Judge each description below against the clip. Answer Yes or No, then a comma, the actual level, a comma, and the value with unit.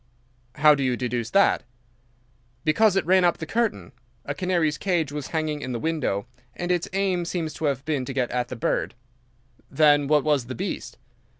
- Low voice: No, medium, 150 Hz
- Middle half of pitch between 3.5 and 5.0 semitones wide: Yes, average, 4.6 semitones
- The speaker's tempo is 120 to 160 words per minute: No, average, 190 wpm